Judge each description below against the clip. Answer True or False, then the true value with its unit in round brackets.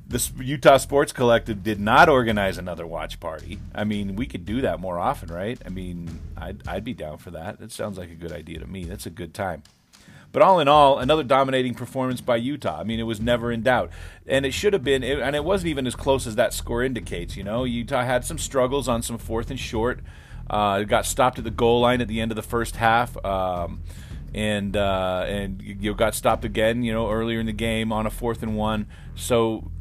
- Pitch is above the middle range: False (110 Hz)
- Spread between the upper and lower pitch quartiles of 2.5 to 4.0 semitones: False (4.5 semitones)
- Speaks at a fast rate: True (240 wpm)